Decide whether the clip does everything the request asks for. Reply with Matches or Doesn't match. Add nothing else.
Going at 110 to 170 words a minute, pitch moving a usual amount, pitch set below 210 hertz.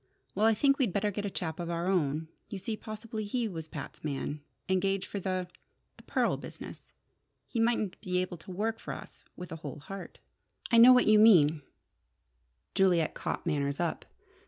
Doesn't match